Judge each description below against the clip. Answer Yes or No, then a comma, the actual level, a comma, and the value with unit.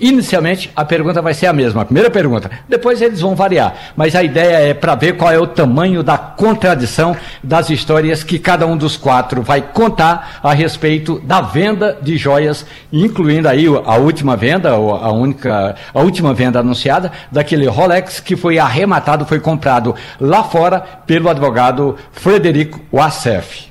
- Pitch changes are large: No, average, 4.1 semitones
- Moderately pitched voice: Yes, medium, 155 Hz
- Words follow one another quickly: No, average, 165 wpm